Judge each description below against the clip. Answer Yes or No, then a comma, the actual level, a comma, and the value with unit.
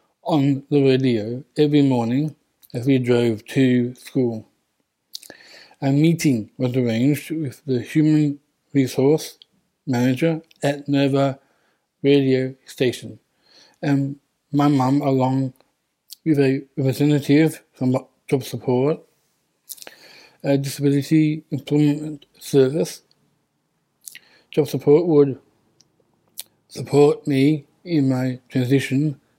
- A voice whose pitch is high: No, medium, 140 Hz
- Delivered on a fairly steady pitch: Yes, narrow, 2.3 semitones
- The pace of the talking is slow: Yes, slow, 90 wpm